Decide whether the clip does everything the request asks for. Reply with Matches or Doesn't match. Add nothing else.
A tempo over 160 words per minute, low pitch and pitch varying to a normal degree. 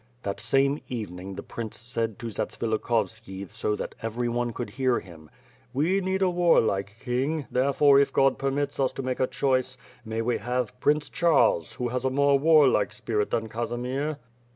Matches